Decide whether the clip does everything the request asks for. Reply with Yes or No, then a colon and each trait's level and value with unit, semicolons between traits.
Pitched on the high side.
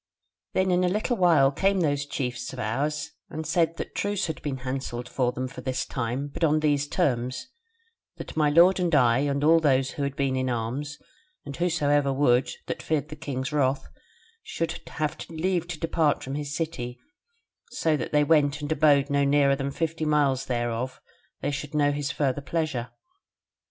No: medium, 145 Hz